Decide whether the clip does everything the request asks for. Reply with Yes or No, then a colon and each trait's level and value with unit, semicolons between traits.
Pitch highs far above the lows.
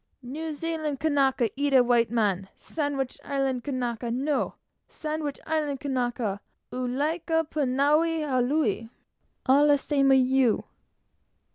No: average, 3.2 semitones